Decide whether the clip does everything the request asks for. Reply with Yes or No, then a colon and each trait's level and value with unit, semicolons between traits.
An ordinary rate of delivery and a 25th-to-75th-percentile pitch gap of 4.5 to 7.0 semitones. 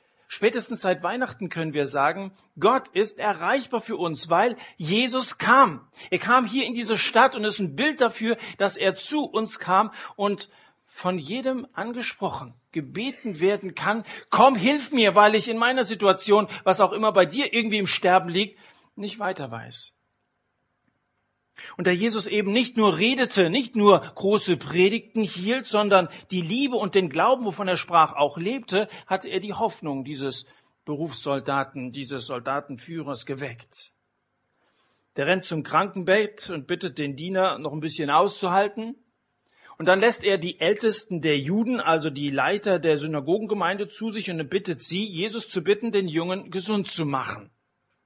Yes: average, 160 wpm; average, 4.8 semitones